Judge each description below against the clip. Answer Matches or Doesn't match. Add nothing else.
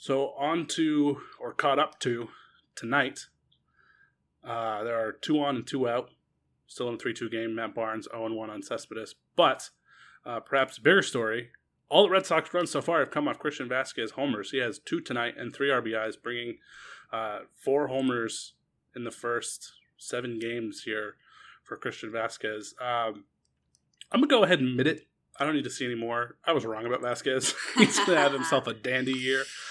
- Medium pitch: Doesn't match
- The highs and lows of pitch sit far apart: Doesn't match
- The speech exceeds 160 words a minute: Matches